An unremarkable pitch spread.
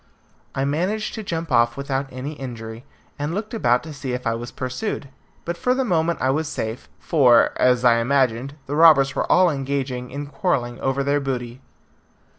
Yes: average, 4.1 semitones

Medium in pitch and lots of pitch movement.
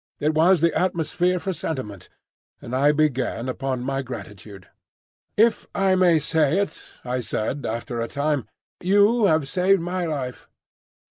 Yes: medium, 155 Hz; wide, 5.8 semitones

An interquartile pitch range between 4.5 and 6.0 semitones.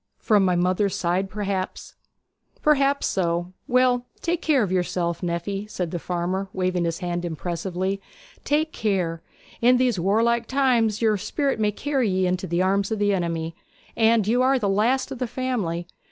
Yes: average, 5.1 semitones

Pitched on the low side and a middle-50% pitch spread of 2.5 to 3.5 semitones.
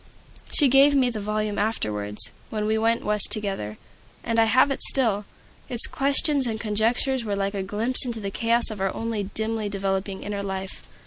No: high, 215 Hz; average, 2.9 semitones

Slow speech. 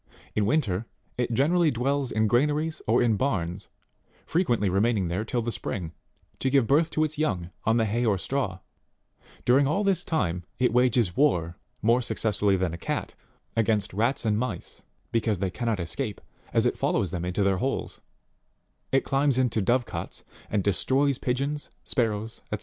No: average, 170 wpm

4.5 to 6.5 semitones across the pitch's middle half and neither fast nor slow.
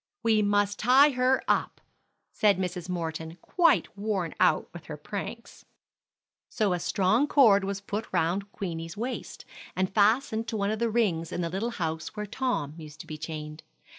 Yes: average, 5.0 semitones; average, 170 wpm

